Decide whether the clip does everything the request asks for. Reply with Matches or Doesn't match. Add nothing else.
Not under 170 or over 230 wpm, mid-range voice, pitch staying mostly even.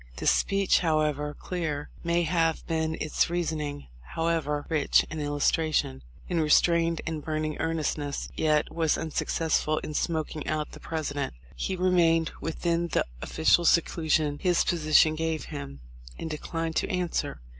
Doesn't match